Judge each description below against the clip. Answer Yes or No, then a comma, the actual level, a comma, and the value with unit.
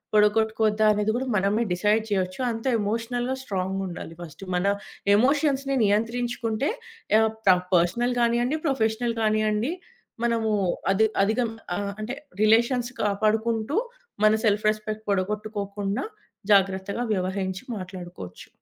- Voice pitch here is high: Yes, high, 215 Hz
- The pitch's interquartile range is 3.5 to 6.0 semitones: No, average, 2.8 semitones